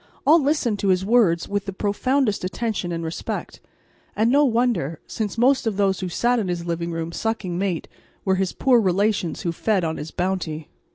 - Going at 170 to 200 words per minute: Yes, average, 190 wpm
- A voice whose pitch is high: Yes, high, 195 Hz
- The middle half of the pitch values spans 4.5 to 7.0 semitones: Yes, average, 4.8 semitones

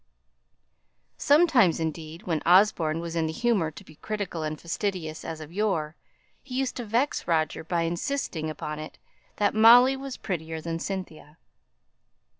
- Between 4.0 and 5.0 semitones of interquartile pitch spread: No, wide, 5.4 semitones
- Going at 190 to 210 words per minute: No, average, 150 wpm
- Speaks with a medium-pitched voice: Yes, medium, 170 Hz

